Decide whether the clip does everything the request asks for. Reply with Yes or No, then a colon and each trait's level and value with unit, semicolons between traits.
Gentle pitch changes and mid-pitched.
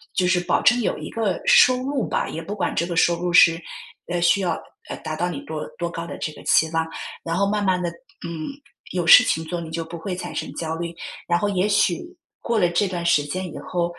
Yes: narrow, 2.3 semitones; medium, 175 Hz